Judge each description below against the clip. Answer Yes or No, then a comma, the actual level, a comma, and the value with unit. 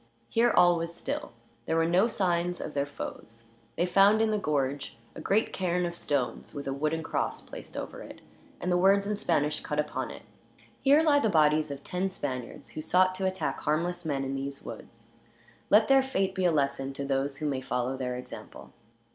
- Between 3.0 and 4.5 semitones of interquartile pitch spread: No, average, 5.3 semitones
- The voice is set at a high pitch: No, medium, 165 Hz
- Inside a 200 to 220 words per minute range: Yes, fast, 205 wpm